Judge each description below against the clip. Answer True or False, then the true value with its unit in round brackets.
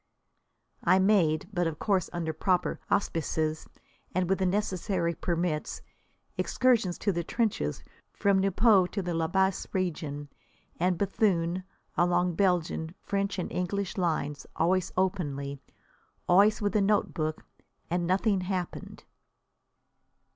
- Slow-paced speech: True (120 wpm)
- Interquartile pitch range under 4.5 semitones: True (2.8 semitones)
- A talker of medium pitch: True (180 Hz)